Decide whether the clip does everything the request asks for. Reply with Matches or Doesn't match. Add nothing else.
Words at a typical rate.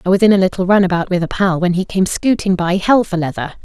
Doesn't match